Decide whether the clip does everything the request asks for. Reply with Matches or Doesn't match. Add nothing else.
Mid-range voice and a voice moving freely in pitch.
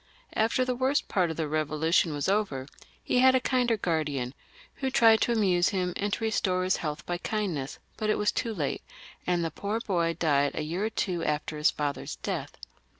Matches